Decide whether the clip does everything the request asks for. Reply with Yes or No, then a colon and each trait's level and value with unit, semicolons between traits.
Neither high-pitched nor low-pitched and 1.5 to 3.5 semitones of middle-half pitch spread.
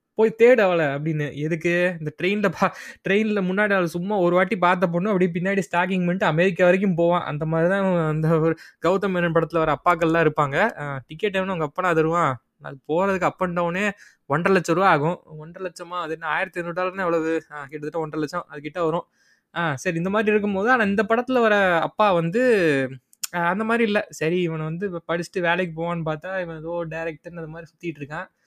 Yes: medium, 175 Hz; average, 2.9 semitones